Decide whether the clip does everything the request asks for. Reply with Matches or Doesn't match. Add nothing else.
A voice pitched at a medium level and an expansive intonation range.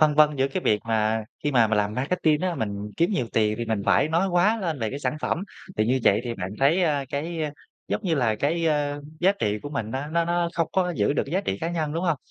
Matches